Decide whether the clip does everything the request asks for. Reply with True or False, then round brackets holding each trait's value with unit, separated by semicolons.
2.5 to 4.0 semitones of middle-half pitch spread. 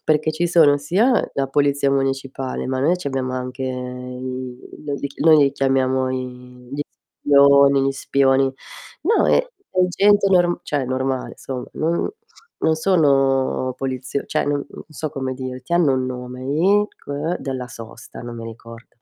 True (2.9 semitones)